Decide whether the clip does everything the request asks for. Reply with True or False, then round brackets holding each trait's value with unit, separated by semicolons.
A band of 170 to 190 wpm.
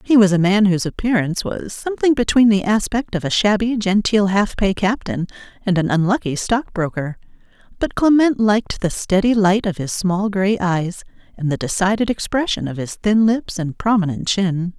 True (180 wpm)